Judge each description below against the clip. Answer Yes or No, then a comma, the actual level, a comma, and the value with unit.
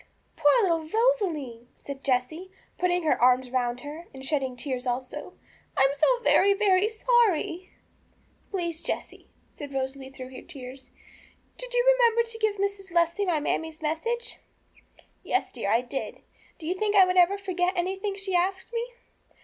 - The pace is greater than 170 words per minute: No, average, 160 wpm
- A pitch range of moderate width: No, wide, 6.9 semitones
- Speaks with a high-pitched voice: Yes, very high, 345 Hz